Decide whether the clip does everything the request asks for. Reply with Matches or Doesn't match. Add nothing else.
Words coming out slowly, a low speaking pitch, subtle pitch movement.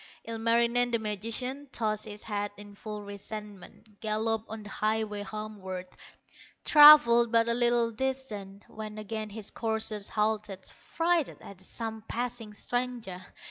Doesn't match